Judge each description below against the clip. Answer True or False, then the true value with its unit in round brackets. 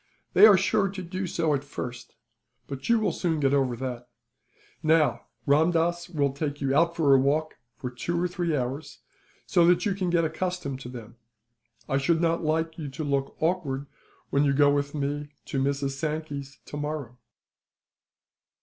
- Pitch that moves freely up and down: False (3.6 semitones)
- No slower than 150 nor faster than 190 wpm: True (175 wpm)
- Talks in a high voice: False (150 Hz)